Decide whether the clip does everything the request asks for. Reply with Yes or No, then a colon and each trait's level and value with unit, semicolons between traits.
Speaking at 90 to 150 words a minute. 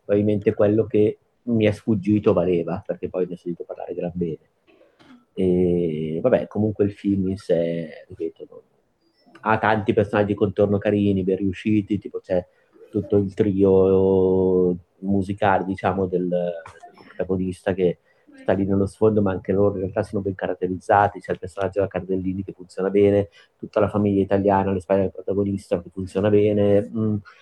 No: average, 165 wpm